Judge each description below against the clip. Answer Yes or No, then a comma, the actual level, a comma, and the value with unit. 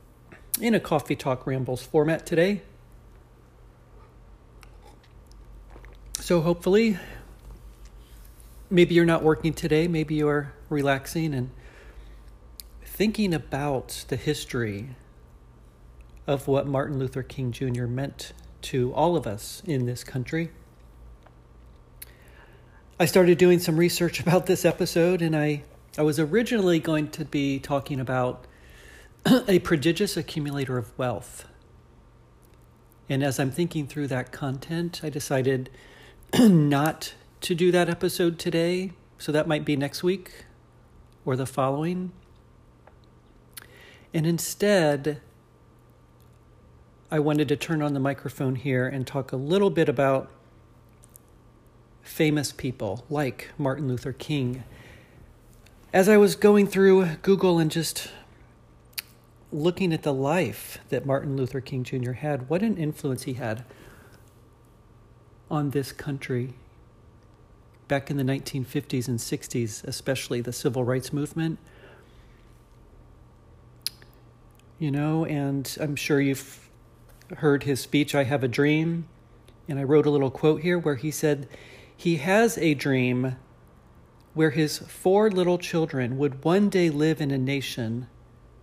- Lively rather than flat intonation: No, average, 4.6 semitones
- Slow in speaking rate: Yes, slow, 125 wpm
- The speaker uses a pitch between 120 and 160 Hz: Yes, medium, 140 Hz